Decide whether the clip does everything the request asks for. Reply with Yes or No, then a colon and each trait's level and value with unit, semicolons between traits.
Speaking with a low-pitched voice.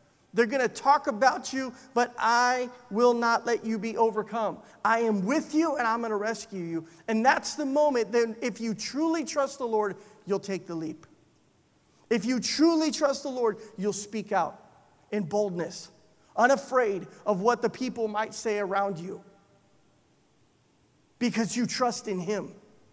No: high, 225 Hz